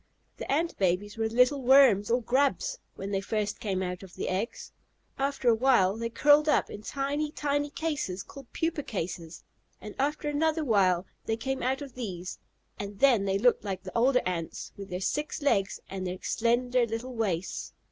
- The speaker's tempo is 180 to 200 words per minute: Yes, average, 185 wpm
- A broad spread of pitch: Yes, wide, 6.0 semitones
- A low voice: No, high, 230 Hz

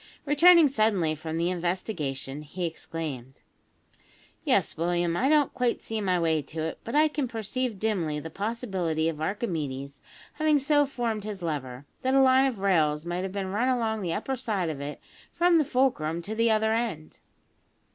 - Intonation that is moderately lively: No, wide, 7.3 semitones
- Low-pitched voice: No, high, 195 Hz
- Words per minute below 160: No, average, 175 wpm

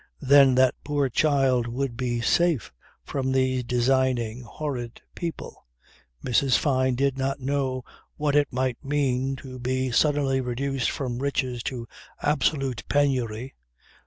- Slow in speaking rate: Yes, slow, 130 wpm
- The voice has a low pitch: Yes, low, 130 Hz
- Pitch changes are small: Yes, narrow, 2.0 semitones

